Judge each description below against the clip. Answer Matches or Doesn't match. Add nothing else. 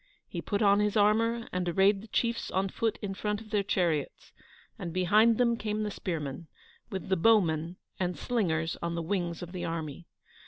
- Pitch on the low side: Doesn't match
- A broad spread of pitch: Doesn't match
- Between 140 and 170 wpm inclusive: Doesn't match